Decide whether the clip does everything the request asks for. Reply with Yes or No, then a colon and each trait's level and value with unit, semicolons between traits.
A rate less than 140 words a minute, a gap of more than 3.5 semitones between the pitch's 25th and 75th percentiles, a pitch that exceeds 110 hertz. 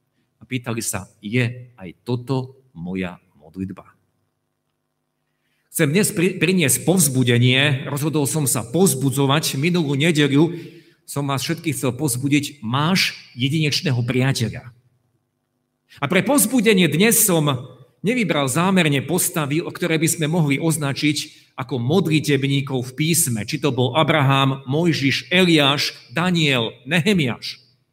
Yes: slow, 110 wpm; average, 4.3 semitones; medium, 140 Hz